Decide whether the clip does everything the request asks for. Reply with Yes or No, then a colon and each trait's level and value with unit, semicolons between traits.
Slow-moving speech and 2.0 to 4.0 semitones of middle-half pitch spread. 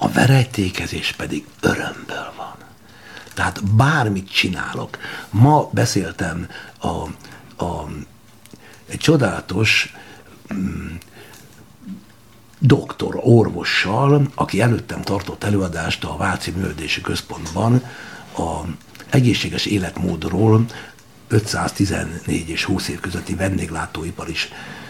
No: slow, 85 wpm; average, 4.5 semitones